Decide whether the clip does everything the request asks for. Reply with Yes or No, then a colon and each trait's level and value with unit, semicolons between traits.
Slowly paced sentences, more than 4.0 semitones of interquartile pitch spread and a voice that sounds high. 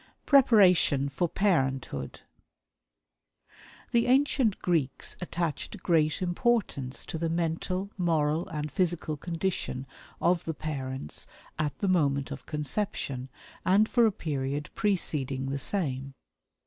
No: slow, 110 wpm; average, 5.2 semitones; medium, 160 Hz